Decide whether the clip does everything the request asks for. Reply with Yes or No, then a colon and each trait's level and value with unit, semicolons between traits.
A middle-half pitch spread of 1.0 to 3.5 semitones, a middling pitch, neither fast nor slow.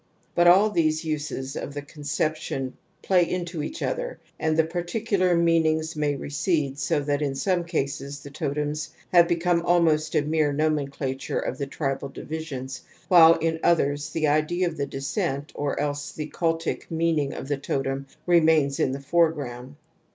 Yes: average, 2.9 semitones; medium, 155 Hz; average, 160 wpm